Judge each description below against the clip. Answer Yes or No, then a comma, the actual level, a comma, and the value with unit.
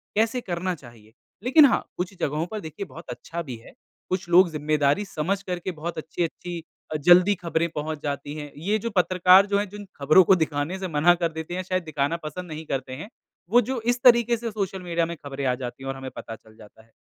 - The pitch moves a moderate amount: Yes, average, 4.5 semitones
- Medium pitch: Yes, medium, 170 Hz